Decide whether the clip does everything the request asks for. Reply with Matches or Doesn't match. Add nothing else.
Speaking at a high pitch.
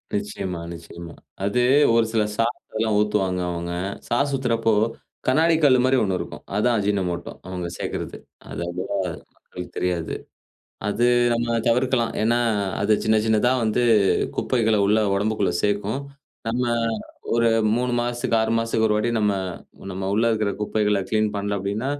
Doesn't match